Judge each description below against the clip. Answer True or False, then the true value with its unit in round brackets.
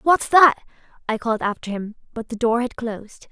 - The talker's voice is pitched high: True (235 Hz)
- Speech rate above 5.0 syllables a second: True (5.5 syllables/s)